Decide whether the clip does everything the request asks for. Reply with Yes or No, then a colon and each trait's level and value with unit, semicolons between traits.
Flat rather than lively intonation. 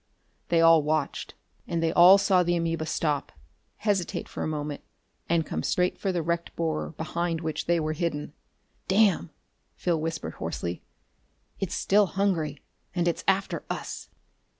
Yes: narrow, 2.3 semitones